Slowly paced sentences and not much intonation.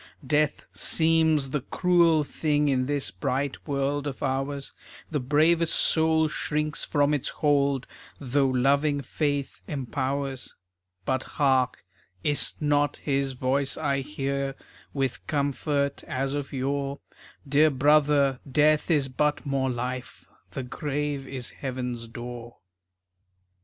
Yes: slow, 120 wpm; narrow, 1.9 semitones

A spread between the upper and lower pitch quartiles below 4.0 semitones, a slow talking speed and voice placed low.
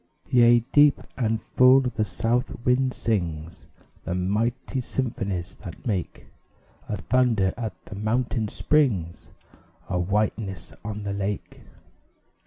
No: average, 4.3 semitones; slow, 115 wpm; low, 110 Hz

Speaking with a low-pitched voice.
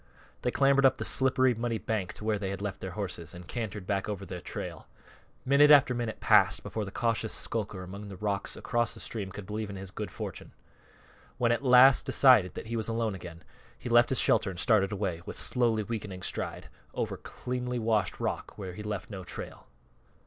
Yes: low, 105 Hz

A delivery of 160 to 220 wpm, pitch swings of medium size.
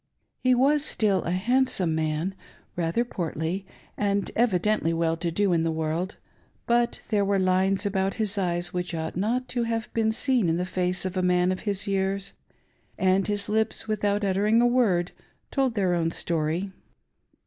Yes: average, 170 wpm; average, 3.7 semitones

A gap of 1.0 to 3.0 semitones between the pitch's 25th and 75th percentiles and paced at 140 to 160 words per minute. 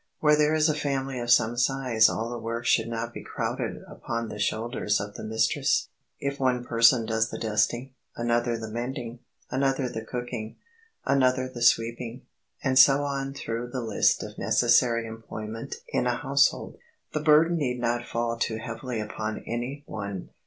No: average, 2.7 semitones; average, 170 wpm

